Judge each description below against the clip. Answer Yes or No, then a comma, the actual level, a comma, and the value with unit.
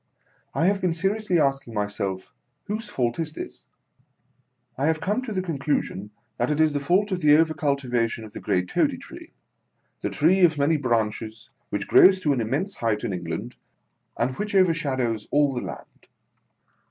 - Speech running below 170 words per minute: No, average, 180 wpm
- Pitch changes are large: Yes, wide, 7.2 semitones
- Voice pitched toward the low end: No, medium, 145 Hz